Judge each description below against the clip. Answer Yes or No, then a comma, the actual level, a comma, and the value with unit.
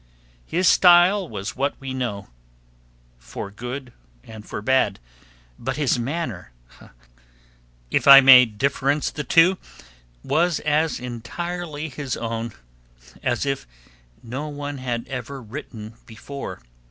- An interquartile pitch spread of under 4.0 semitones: No, average, 4.3 semitones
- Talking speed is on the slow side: Yes, slow, 115 wpm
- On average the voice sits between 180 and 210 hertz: No, low, 135 Hz